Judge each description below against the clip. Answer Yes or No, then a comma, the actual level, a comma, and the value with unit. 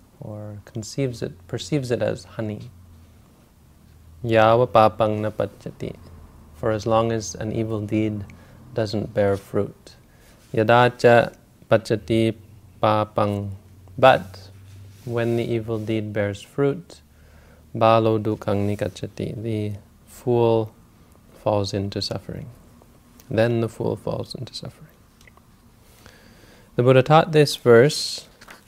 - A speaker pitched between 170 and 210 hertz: No, low, 110 Hz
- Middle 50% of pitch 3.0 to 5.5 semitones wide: No, narrow, 2.5 semitones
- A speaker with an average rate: No, slow, 100 wpm